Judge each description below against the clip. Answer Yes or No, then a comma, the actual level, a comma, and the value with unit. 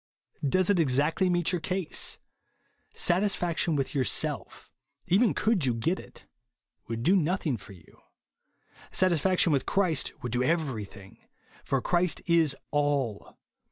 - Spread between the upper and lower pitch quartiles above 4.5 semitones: Yes, wide, 5.6 semitones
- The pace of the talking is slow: Yes, slow, 125 wpm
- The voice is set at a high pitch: No, medium, 160 Hz